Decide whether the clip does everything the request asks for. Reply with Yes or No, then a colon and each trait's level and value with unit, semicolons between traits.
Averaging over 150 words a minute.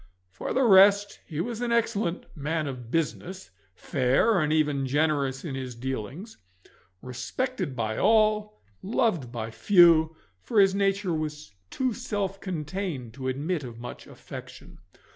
No: average, 145 wpm